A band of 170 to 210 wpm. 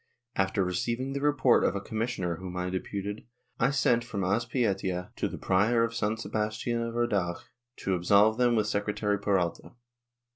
No: average, 160 wpm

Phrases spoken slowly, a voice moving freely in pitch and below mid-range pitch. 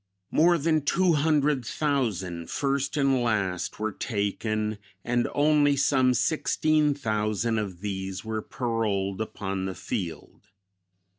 Yes: slow, 120 wpm; wide, 6.2 semitones; low, 115 Hz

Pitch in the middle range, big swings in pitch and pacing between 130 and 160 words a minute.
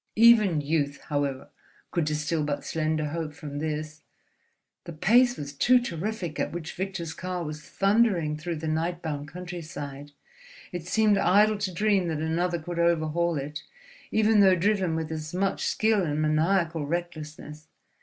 No: medium, 165 Hz; average, 3.6 semitones; average, 155 wpm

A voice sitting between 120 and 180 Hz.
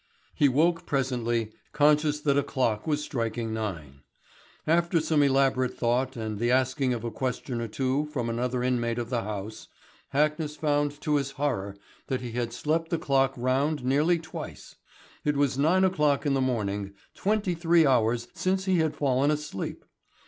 Yes: low, 135 Hz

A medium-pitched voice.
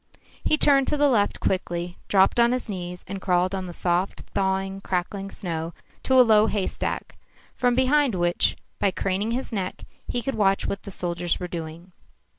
No: high, 195 Hz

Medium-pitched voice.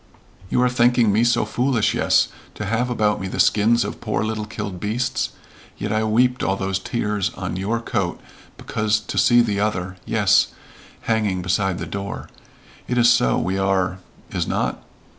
No: low, 105 Hz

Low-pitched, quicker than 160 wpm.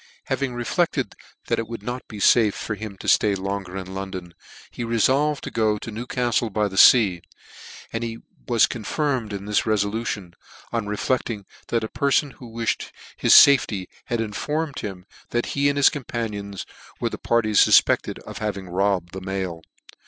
Yes: low, 110 Hz; average, 170 wpm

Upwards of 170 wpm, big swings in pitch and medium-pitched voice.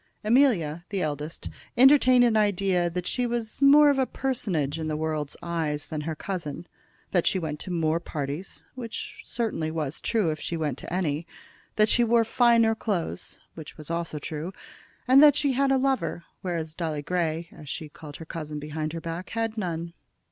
Yes: average, 185 wpm; wide, 6.6 semitones; medium, 170 Hz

